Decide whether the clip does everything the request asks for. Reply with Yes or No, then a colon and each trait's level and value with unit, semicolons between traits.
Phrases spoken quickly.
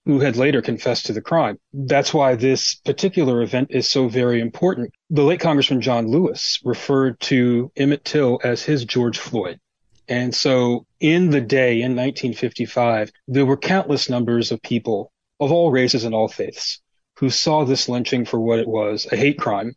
No: average, 180 wpm